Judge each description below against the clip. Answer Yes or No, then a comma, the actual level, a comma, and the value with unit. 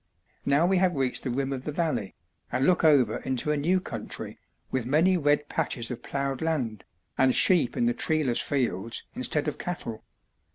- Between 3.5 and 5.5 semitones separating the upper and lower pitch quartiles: Yes, average, 4.2 semitones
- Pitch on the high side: No, medium, 140 Hz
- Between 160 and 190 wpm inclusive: Yes, average, 180 wpm